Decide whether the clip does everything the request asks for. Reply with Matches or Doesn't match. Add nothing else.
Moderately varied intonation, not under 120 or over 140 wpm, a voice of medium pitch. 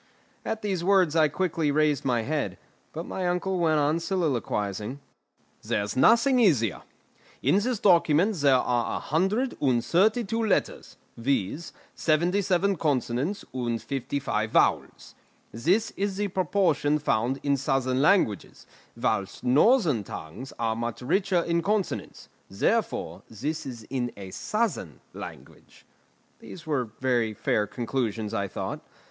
Doesn't match